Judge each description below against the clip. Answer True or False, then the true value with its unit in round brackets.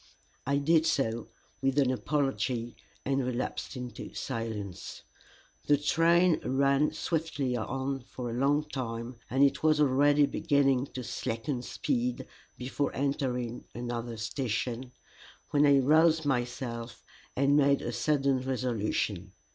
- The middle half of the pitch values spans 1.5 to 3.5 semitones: True (2.9 semitones)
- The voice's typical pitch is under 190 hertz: True (135 Hz)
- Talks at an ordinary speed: False (125 wpm)